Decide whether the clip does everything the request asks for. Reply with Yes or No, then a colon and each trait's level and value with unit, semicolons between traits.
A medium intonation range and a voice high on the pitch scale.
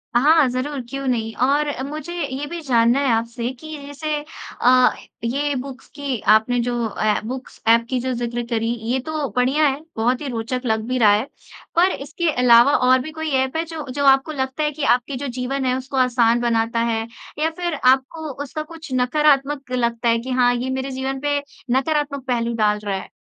Yes: average, 3.2 semitones; very high, 260 Hz